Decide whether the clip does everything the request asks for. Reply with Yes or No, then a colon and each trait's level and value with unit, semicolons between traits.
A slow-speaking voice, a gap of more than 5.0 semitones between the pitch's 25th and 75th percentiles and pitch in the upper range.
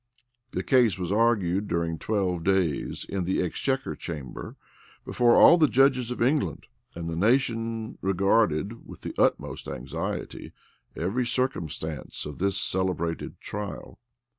No: slow, 130 wpm; wide, 5.6 semitones; low, 100 Hz